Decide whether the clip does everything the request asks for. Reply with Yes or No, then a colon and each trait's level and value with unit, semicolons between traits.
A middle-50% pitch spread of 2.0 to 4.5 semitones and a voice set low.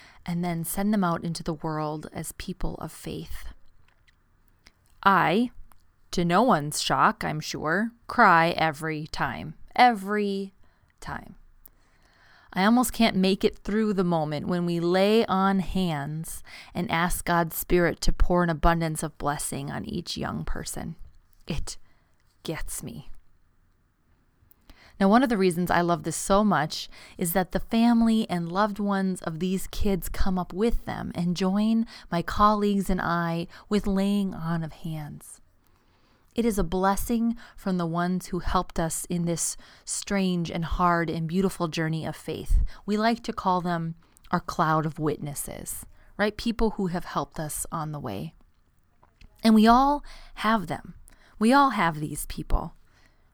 No: average, 4.2 semitones; medium, 180 Hz